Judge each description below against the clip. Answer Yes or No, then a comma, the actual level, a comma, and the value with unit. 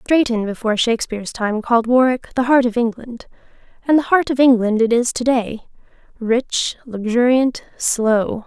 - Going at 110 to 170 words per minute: Yes, average, 140 wpm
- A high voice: Yes, high, 240 Hz